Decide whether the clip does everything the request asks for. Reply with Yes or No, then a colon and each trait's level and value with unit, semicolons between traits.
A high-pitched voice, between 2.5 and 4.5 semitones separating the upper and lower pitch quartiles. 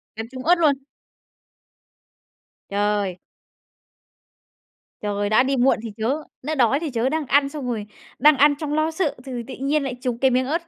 Yes: very high, 265 Hz; average, 4.2 semitones